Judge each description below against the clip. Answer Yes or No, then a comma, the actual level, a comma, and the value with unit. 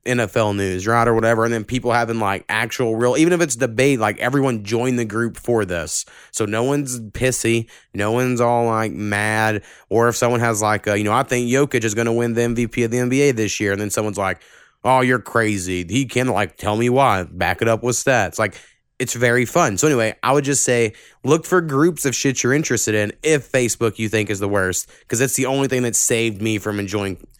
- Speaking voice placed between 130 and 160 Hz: No, low, 115 Hz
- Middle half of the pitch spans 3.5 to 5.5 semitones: No, average, 2.9 semitones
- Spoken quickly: Yes, fast, 230 wpm